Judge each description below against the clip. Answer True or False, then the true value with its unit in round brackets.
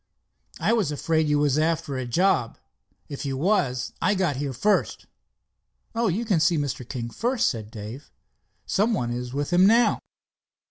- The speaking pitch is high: False (150 Hz)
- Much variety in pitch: True (7.1 semitones)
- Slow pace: False (170 wpm)